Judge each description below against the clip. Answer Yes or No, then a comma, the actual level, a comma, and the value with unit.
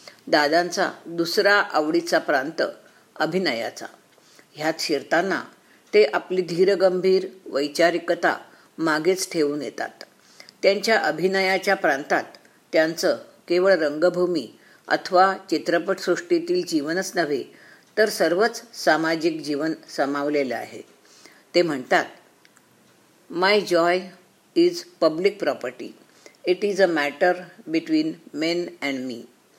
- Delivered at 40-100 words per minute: Yes, average, 90 wpm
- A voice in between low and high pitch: Yes, medium, 180 Hz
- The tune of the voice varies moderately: Yes, average, 3.6 semitones